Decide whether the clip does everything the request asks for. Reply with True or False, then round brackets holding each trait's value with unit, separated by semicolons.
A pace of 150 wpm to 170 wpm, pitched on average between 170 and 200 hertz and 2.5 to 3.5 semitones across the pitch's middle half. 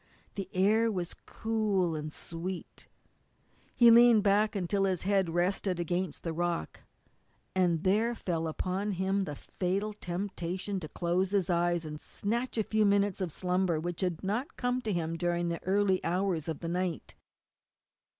True (160 wpm; 185 Hz; 2.8 semitones)